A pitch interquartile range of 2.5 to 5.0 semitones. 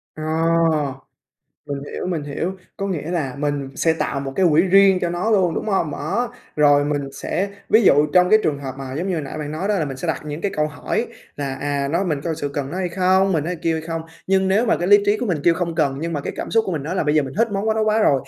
Yes: average, 4.7 semitones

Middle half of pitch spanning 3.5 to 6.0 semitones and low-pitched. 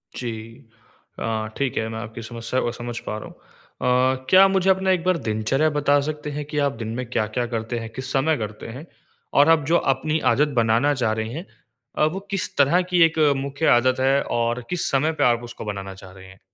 Yes: average, 4.8 semitones; low, 130 Hz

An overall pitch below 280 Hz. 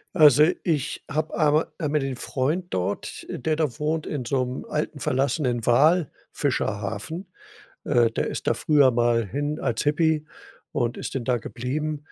Yes: medium, 140 Hz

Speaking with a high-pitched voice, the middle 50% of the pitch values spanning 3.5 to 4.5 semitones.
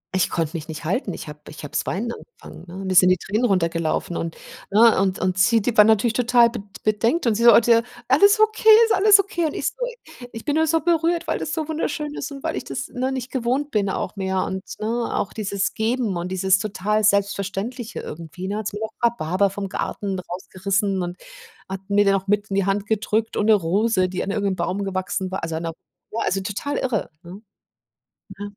Yes: high, 205 Hz; average, 4.2 semitones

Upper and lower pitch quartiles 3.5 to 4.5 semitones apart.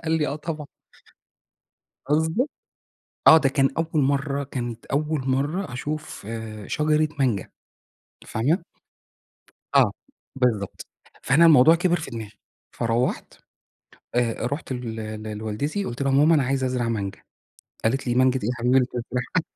Yes: average, 4.2 semitones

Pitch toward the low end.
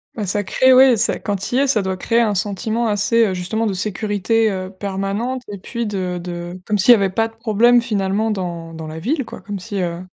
No: high, 205 Hz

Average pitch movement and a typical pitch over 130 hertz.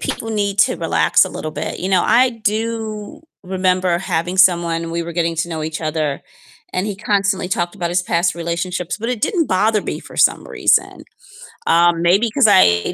Yes: average, 3.6 semitones; medium, 185 Hz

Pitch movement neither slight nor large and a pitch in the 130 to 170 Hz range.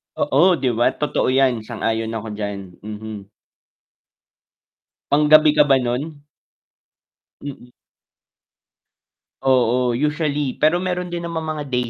Yes: average, 4.2 semitones; low, 135 Hz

